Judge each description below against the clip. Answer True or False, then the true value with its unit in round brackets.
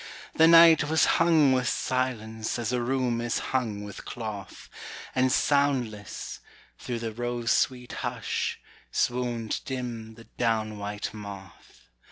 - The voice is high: False (120 Hz)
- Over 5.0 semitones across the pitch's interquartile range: False (3.0 semitones)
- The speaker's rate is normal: False (130 wpm)